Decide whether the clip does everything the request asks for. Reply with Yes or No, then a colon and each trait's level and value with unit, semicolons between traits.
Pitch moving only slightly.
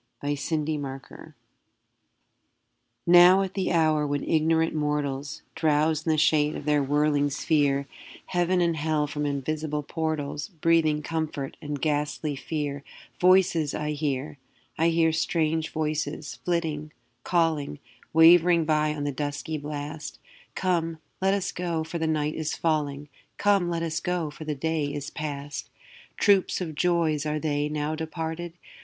Yes: narrow, 1.9 semitones